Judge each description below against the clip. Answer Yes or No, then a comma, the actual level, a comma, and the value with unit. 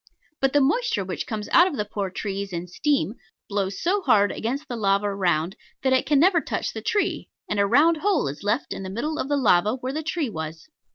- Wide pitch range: Yes, wide, 7.1 semitones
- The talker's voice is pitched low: No, high, 225 Hz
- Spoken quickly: Yes, fast, 230 wpm